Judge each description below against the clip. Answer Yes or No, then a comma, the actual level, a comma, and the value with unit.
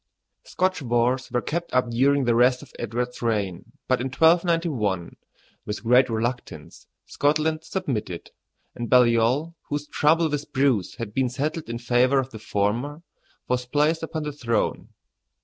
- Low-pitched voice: Yes, low, 125 Hz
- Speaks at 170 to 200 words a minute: No, average, 150 wpm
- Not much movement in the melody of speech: No, average, 4.1 semitones